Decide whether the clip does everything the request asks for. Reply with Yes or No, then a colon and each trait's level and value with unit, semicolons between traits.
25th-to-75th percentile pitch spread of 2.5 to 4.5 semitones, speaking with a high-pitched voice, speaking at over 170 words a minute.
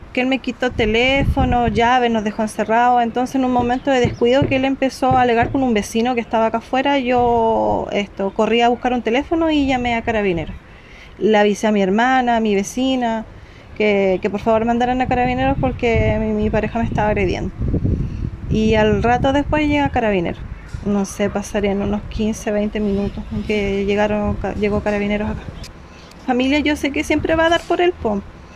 Yes: average, 3.5 semitones; high, 230 Hz; average, 185 wpm